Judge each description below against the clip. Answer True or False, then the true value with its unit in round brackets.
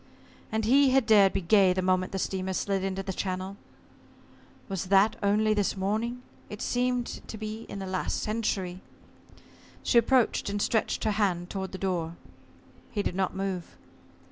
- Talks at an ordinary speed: True (170 wpm)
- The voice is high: True (195 Hz)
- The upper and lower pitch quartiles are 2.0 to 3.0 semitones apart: True (2.5 semitones)